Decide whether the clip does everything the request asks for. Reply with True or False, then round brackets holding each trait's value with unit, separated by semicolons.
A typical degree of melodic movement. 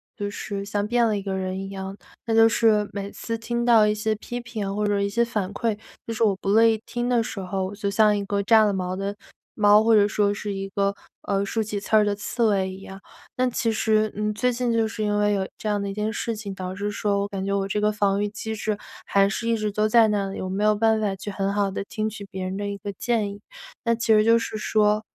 False (1.8 semitones)